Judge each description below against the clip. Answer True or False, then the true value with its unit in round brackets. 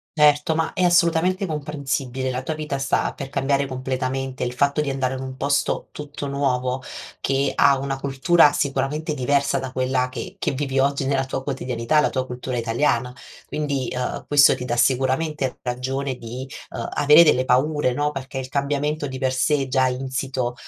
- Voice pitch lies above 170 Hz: False (135 Hz)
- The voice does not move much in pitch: True (2.1 semitones)